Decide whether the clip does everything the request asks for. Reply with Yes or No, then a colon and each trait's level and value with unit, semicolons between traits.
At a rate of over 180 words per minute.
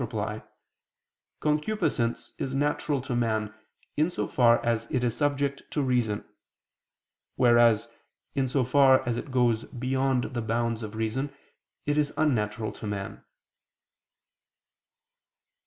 No: slow, 135 wpm